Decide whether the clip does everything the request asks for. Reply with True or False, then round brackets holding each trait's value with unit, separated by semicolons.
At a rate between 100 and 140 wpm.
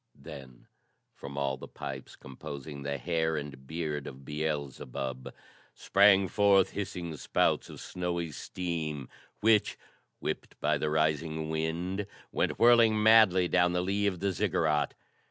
True (135 wpm)